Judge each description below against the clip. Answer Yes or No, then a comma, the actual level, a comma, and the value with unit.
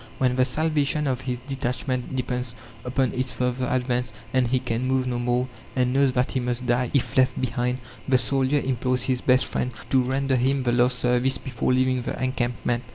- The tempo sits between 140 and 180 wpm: No, average, 195 wpm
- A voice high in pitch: No, low, 125 Hz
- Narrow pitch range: Yes, narrow, 1.1 semitones